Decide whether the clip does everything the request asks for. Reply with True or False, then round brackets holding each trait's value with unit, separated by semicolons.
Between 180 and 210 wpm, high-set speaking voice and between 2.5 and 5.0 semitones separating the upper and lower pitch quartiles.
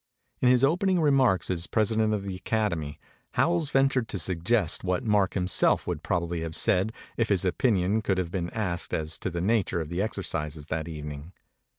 False (185 wpm; 95 Hz; 4.6 semitones)